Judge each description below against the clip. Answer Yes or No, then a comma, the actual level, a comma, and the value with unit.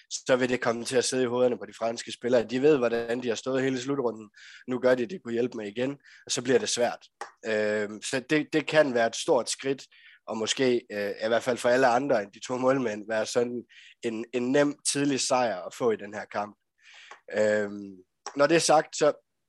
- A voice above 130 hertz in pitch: No, low, 125 Hz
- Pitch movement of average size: Yes, average, 3.0 semitones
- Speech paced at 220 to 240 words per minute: Yes, fast, 225 wpm